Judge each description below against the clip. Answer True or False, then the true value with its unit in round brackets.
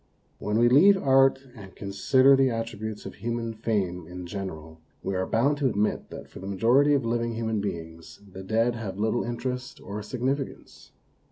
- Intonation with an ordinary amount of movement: True (4.4 semitones)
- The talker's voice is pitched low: True (115 Hz)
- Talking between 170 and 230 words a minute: True (180 wpm)